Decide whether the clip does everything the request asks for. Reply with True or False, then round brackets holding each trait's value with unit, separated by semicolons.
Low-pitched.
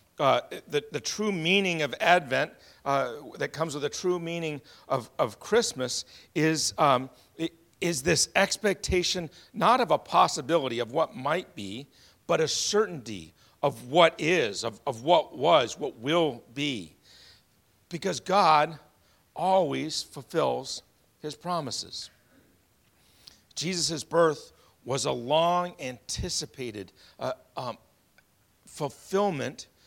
False (150 Hz)